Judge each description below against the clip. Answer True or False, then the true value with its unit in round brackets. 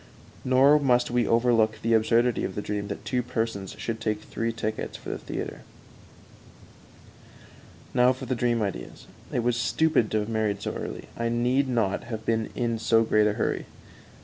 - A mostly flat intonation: True (2.0 semitones)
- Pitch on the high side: False (115 Hz)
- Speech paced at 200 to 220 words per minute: False (175 wpm)